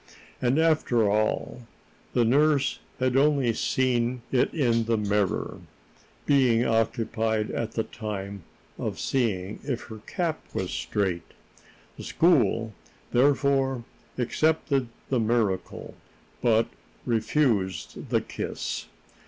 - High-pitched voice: No, low, 120 Hz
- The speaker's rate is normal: No, slow, 105 wpm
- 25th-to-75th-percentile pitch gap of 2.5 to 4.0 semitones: Yes, average, 3.5 semitones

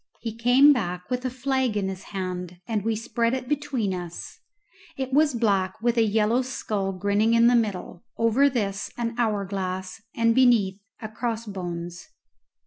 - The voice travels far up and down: No, average, 4.1 semitones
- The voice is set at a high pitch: Yes, high, 225 Hz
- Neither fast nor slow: Yes, average, 165 wpm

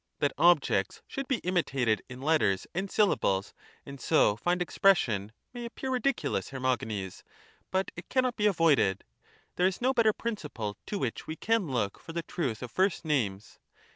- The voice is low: No, medium, 160 Hz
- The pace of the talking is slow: No, average, 170 wpm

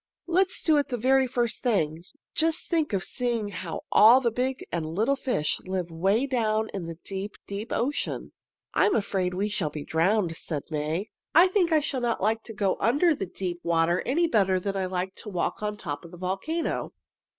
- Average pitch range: No, wide, 6.2 semitones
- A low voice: No, high, 210 Hz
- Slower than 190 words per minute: No, fast, 205 wpm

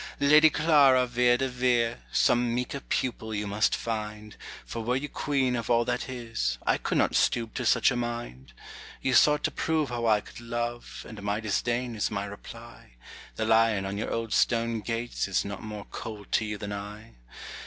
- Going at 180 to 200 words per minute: Yes, average, 190 wpm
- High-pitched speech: No, low, 115 Hz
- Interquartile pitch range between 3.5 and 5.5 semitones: No, narrow, 2.6 semitones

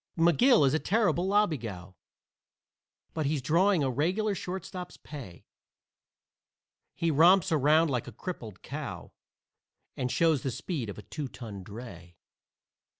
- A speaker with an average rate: No, slow, 130 wpm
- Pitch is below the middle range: No, medium, 150 Hz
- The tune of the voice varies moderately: No, wide, 6.6 semitones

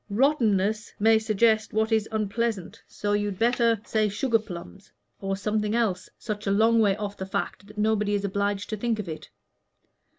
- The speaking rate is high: No, average, 175 wpm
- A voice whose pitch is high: Yes, high, 210 Hz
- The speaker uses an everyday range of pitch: No, narrow, 1.6 semitones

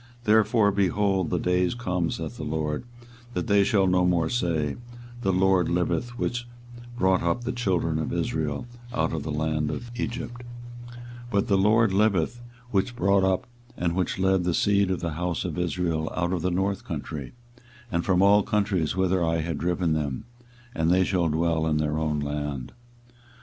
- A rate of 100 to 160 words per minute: No, average, 180 wpm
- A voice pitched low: Yes, very low, 90 Hz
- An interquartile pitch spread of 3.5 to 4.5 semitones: Yes, average, 3.8 semitones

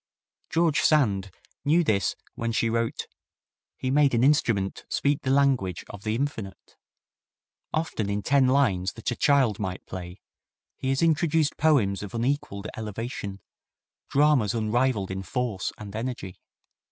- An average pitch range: No, wide, 5.9 semitones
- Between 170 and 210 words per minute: No, average, 140 wpm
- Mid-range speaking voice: No, low, 115 Hz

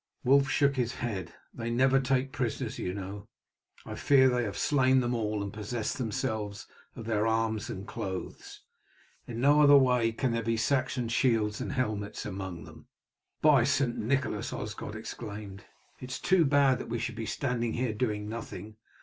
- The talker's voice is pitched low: Yes, low, 115 Hz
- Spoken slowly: No, average, 175 wpm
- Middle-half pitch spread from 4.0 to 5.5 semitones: No, average, 3.6 semitones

